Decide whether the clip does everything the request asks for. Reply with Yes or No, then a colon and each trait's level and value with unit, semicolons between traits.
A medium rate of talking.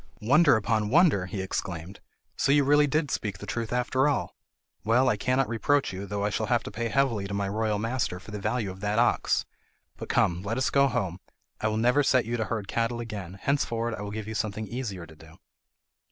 No: fast, 225 wpm